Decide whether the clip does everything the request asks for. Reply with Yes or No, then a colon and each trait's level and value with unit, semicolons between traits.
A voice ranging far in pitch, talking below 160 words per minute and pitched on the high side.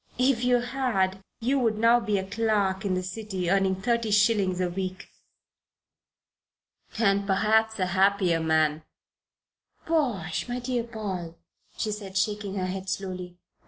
No: average, 3.4 semitones; average, 140 wpm; high, 200 Hz